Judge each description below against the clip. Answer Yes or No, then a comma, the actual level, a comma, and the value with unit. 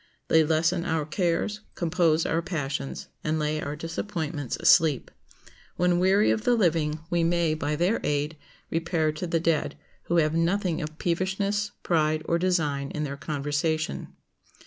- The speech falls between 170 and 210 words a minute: No, average, 150 wpm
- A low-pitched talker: No, medium, 165 Hz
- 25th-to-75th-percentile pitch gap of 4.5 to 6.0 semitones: No, narrow, 2.4 semitones